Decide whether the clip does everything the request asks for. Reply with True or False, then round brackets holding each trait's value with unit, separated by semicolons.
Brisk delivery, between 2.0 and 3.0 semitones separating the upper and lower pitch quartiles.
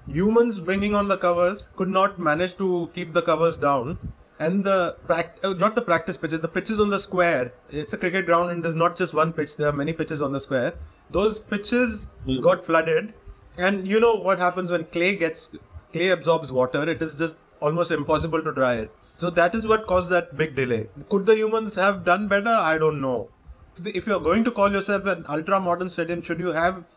False (210 wpm; 3.6 semitones)